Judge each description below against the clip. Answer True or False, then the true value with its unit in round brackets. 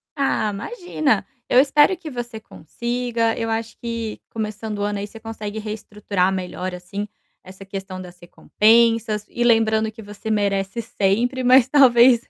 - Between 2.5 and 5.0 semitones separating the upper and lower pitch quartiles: True (2.8 semitones)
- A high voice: True (220 Hz)